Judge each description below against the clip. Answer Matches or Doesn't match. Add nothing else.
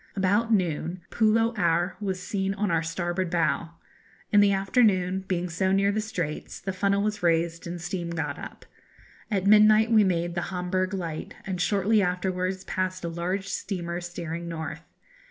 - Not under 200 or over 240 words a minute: Doesn't match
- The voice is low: Doesn't match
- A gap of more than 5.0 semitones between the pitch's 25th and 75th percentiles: Doesn't match